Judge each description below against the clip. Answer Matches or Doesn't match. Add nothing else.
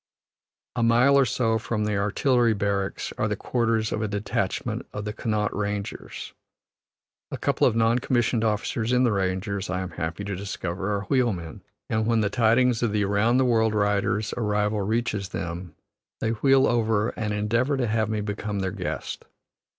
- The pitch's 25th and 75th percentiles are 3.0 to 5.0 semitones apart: Doesn't match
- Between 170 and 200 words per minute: Matches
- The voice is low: Matches